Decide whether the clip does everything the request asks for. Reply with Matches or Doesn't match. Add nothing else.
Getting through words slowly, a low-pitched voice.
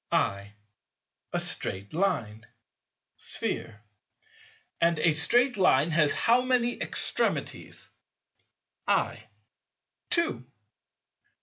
Doesn't match